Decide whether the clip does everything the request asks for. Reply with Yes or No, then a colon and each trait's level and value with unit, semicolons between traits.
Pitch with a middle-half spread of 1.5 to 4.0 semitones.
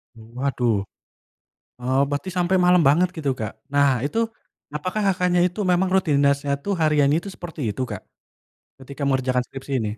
No: average, 5.2 semitones